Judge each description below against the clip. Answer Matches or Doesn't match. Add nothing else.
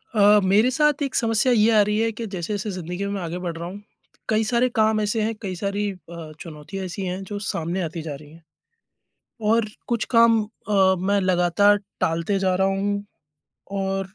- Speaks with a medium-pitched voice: Doesn't match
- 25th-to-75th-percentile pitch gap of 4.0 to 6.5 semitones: Doesn't match